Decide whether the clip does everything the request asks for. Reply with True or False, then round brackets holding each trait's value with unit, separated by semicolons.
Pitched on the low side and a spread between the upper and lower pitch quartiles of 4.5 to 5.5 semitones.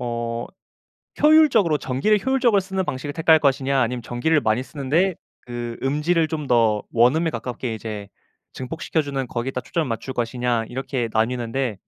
True (130 Hz; 5.1 semitones)